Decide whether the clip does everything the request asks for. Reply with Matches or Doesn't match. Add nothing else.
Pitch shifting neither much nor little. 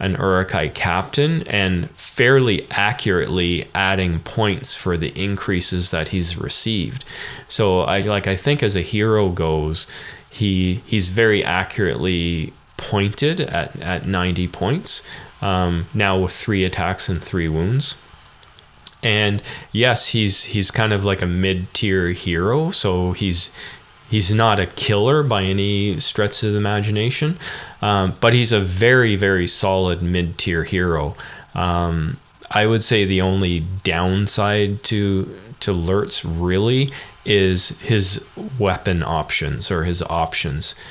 Matches